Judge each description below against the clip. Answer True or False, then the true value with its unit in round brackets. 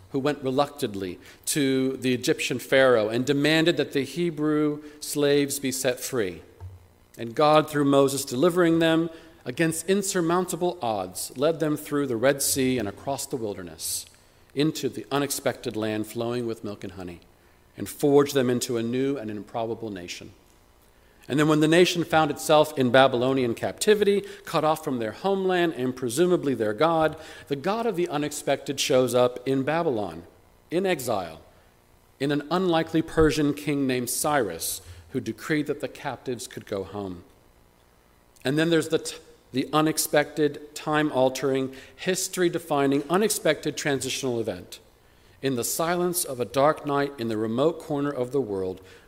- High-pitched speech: False (140 Hz)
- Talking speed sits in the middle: True (155 wpm)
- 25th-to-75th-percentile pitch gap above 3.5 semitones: True (5.3 semitones)